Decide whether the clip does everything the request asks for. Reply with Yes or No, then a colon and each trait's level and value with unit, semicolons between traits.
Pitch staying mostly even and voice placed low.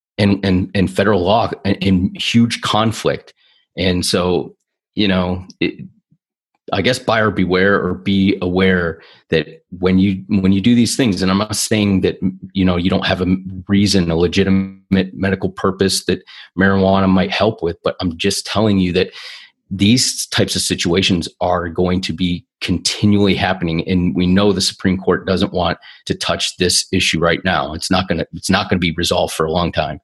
Yes: narrow, 1.6 semitones; very low, 95 Hz